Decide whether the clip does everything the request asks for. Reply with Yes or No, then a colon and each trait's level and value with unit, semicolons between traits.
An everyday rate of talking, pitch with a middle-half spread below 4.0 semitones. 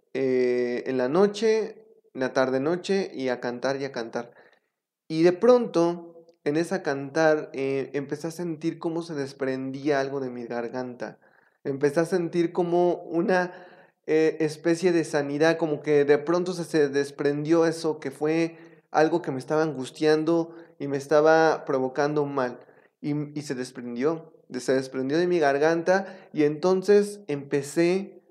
Yes: average, 150 wpm; average, 3.5 semitones